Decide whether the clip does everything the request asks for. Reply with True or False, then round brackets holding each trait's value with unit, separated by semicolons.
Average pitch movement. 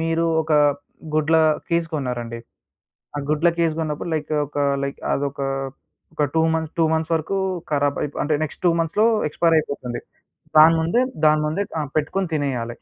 False (2.3 semitones)